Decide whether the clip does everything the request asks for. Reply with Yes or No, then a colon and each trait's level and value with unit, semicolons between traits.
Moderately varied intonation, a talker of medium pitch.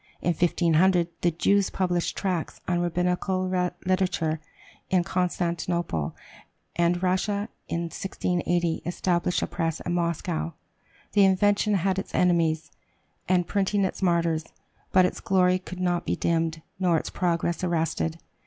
No: narrow, 1.7 semitones; medium, 175 Hz